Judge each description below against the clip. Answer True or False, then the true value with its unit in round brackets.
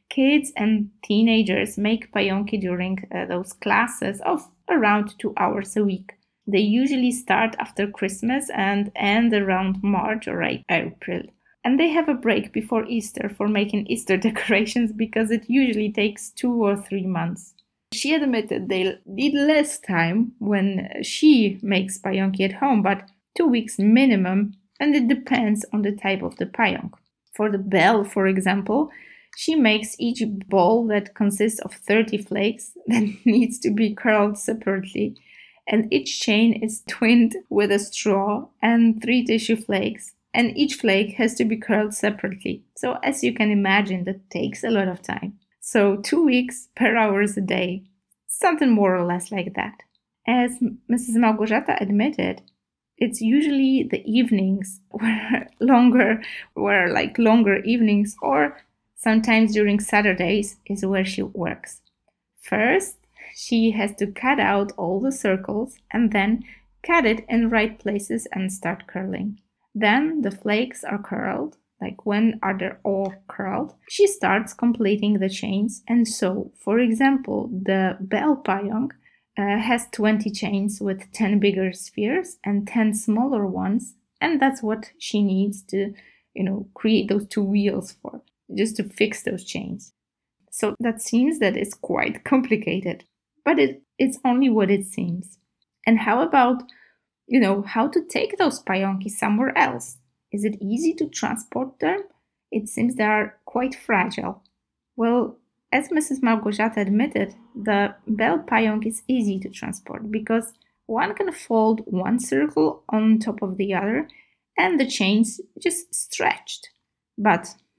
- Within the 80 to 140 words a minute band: False (150 wpm)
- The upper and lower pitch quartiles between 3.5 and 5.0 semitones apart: False (3.1 semitones)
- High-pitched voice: True (215 Hz)